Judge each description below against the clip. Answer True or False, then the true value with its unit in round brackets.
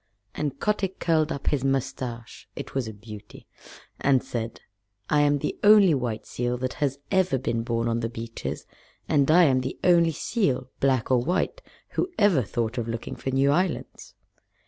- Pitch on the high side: False (135 Hz)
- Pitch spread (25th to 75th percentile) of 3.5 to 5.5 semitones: True (4.8 semitones)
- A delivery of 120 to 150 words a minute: False (175 wpm)